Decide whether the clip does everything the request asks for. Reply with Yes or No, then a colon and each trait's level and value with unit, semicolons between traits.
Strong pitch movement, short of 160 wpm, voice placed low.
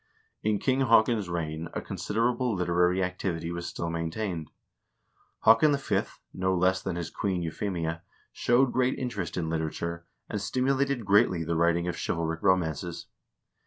No: average, 4.5 semitones; average, 140 wpm; very low, 90 Hz